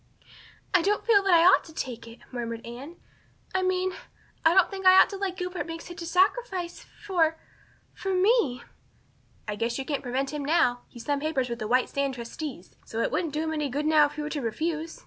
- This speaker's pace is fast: Yes, fast, 225 wpm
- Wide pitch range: Yes, wide, 6.1 semitones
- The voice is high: Yes, very high, 310 Hz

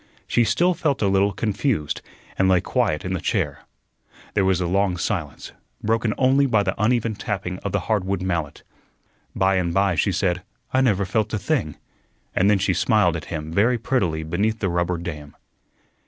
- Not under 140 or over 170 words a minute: No, average, 185 wpm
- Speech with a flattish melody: No, average, 3.8 semitones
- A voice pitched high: No, low, 100 Hz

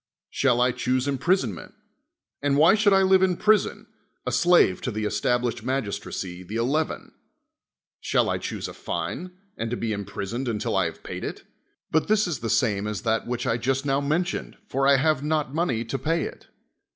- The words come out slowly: No, average, 190 wpm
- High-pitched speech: No, low, 135 Hz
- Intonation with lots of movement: Yes, wide, 5.8 semitones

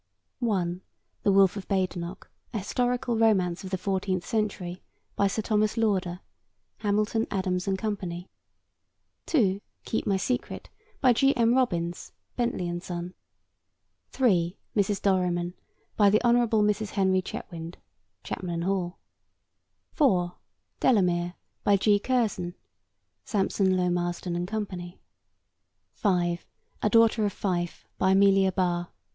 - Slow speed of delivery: Yes, slow, 125 wpm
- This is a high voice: Yes, high, 195 Hz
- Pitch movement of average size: Yes, average, 3.2 semitones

